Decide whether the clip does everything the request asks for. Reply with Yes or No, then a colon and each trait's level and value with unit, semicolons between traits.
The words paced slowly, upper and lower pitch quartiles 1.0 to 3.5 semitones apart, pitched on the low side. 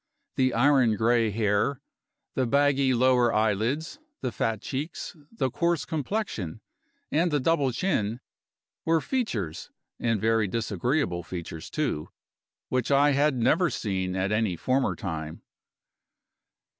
No: slow, 120 wpm; average, 5.3 semitones; low, 125 Hz